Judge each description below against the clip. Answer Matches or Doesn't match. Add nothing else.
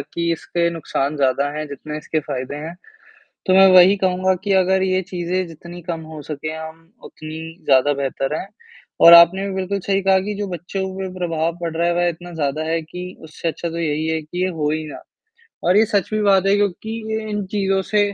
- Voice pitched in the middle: Matches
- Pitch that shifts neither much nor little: Matches